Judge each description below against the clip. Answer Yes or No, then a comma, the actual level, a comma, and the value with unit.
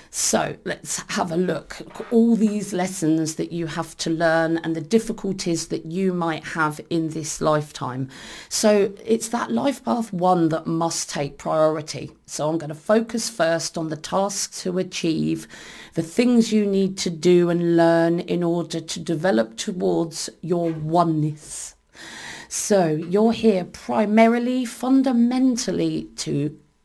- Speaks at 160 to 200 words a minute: No, average, 150 wpm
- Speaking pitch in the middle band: Yes, medium, 170 Hz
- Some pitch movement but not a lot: Yes, average, 4.6 semitones